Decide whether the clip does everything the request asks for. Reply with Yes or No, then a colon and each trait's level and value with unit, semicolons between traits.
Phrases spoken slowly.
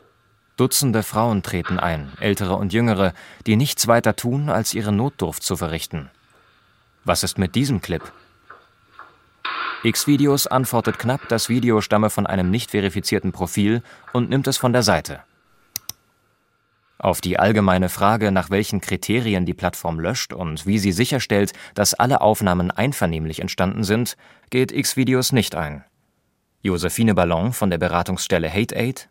No: average, 140 wpm